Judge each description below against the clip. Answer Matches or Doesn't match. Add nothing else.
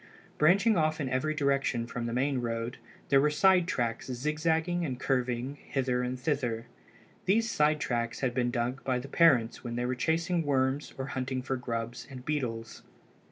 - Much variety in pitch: Doesn't match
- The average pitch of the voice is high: Doesn't match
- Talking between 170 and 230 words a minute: Matches